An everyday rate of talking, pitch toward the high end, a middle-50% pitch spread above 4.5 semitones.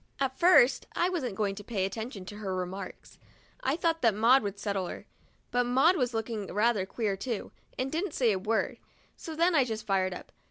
No: fast, 215 wpm; high, 225 Hz; average, 5.1 semitones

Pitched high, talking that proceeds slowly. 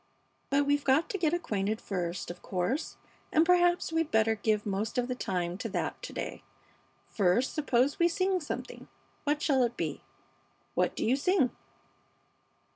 No: very high, 260 Hz; average, 165 wpm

